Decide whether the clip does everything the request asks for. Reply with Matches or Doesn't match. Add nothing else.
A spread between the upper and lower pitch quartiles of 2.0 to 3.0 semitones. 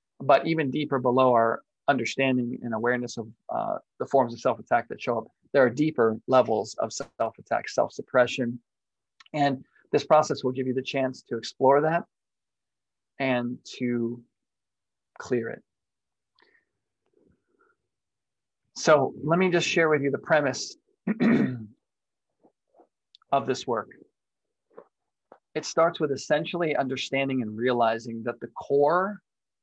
Doesn't match